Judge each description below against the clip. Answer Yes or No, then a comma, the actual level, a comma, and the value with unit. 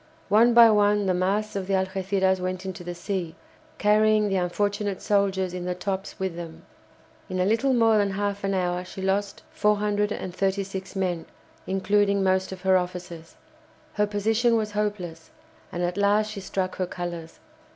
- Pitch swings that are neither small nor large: No, narrow, 2.1 semitones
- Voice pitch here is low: No, high, 195 Hz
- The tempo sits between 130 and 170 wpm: Yes, average, 165 wpm